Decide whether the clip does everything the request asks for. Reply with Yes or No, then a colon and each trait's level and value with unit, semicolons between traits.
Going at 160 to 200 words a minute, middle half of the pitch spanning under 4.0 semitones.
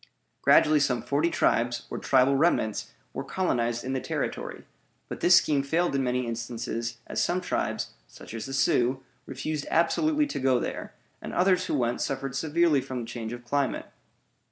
No: average, 175 wpm; average, 4.7 semitones